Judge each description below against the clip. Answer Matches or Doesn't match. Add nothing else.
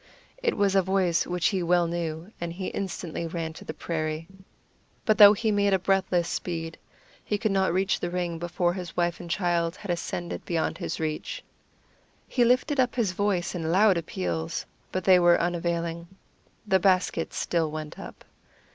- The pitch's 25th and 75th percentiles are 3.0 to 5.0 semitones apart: Doesn't match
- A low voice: Doesn't match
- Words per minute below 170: Doesn't match